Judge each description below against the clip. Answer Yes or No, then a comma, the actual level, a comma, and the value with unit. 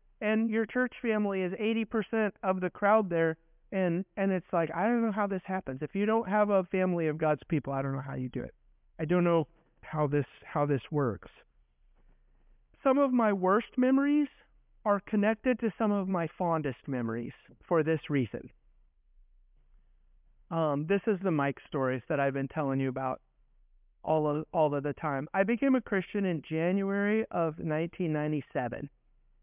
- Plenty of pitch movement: Yes, wide, 6.6 semitones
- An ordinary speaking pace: Yes, average, 175 wpm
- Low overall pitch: No, medium, 165 Hz